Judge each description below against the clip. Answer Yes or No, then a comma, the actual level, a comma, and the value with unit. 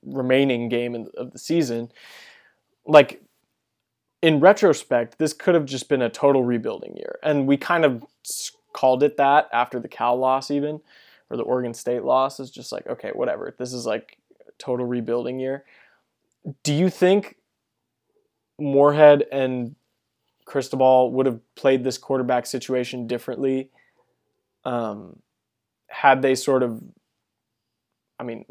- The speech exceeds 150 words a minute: No, average, 140 wpm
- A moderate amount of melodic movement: Yes, average, 3.4 semitones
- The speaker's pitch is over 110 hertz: Yes, low, 135 Hz